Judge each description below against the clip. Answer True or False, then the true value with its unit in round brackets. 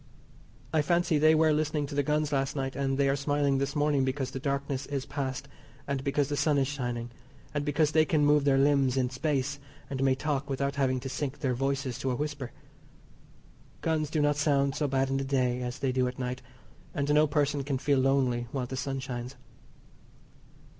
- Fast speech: True (210 wpm)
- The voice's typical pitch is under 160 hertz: True (140 Hz)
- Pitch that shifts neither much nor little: False (1.8 semitones)